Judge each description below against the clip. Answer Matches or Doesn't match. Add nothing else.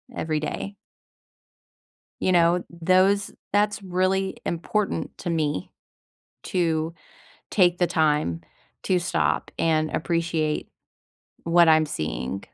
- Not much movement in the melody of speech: Doesn't match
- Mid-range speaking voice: Matches